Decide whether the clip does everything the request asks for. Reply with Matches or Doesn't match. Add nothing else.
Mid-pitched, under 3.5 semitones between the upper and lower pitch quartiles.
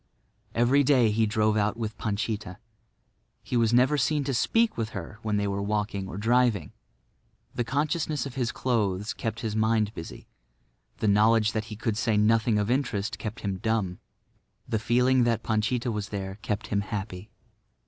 Doesn't match